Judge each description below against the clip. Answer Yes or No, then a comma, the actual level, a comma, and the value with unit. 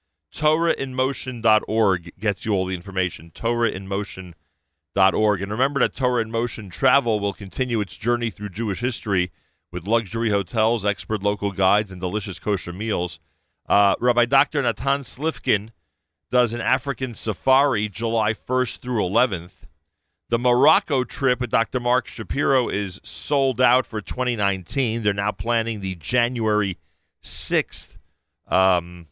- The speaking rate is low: Yes, slow, 130 wpm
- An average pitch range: Yes, average, 4.7 semitones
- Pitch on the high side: No, low, 105 Hz